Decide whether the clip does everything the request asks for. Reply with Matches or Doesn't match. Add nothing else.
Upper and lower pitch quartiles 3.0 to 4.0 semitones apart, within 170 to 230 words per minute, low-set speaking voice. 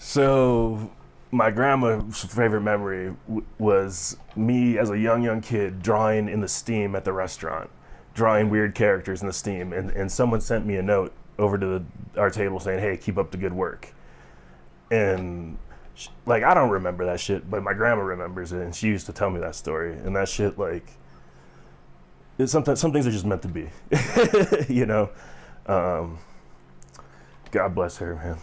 Matches